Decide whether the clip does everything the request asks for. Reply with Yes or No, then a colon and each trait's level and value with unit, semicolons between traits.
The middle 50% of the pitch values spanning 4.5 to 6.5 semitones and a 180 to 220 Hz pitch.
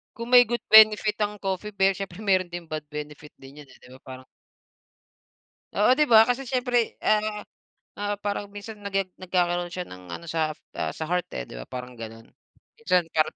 Yes: wide, 5.5 semitones; high, 190 Hz